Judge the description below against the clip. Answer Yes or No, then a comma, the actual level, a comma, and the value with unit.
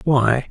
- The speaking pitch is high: No, low, 125 Hz